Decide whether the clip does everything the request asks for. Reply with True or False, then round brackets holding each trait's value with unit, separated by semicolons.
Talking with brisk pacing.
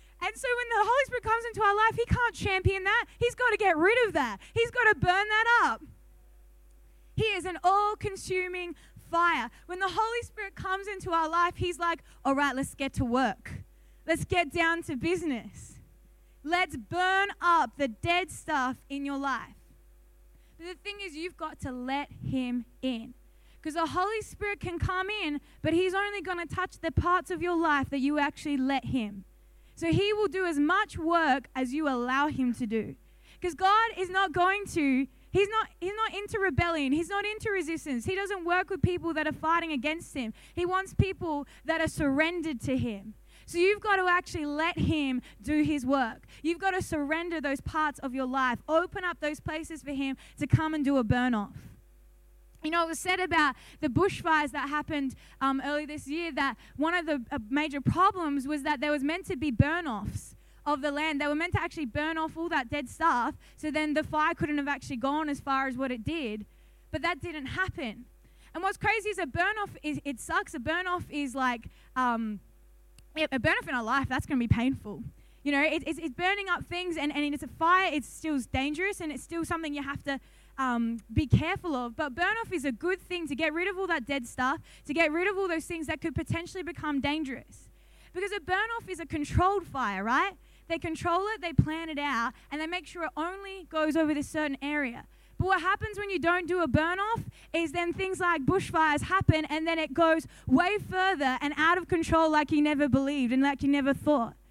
True (215 wpm)